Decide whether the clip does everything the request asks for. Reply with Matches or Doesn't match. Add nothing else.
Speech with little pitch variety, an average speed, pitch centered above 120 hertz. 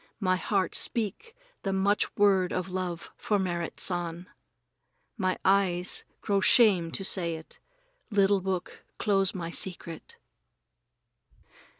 Doesn't match